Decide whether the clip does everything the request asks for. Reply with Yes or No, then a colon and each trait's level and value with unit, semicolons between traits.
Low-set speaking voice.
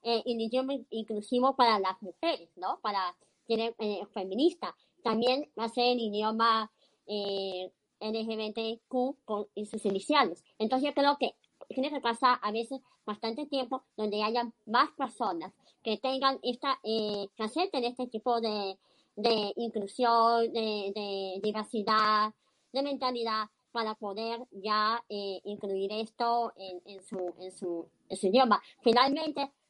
No: high, 225 Hz